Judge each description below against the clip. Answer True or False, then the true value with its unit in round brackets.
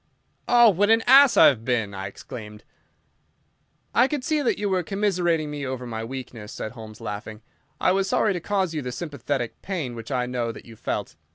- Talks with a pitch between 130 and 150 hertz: True (135 Hz)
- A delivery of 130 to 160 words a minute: False (200 wpm)